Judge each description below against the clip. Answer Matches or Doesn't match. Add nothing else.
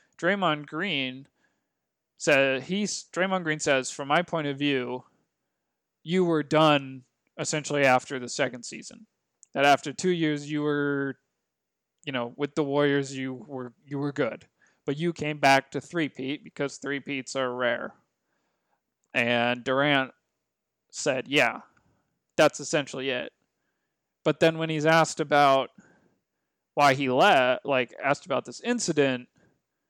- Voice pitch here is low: Doesn't match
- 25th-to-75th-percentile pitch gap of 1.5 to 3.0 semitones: Matches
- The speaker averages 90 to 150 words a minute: Matches